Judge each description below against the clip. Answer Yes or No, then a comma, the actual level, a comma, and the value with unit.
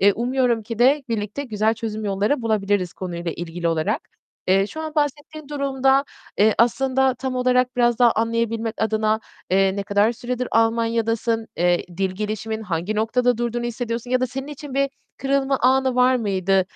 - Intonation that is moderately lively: Yes, average, 3.6 semitones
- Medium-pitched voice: No, high, 230 Hz